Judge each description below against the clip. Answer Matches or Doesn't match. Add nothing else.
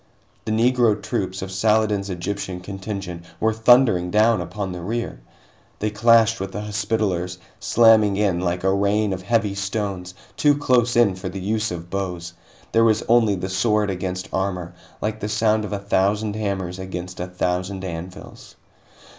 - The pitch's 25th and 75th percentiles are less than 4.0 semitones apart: Matches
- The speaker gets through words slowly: Doesn't match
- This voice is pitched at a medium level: Doesn't match